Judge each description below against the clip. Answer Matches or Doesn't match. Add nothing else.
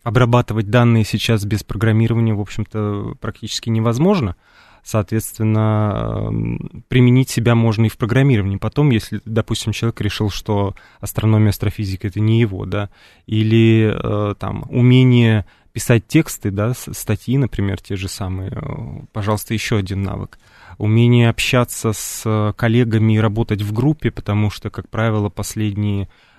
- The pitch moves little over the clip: Matches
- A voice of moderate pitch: Doesn't match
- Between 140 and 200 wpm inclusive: Doesn't match